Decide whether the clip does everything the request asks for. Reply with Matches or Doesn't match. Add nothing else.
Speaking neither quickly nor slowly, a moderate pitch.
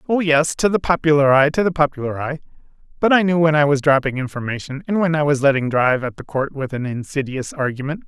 Doesn't match